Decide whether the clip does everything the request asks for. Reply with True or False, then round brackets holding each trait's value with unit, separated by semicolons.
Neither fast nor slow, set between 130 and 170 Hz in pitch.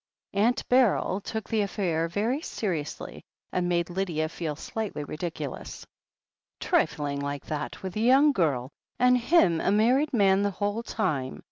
False (160 wpm; 195 Hz)